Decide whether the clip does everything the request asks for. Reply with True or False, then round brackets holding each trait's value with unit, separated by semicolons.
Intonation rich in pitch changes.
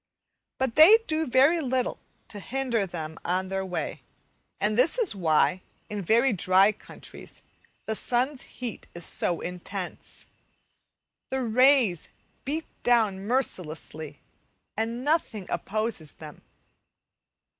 True (6.0 semitones)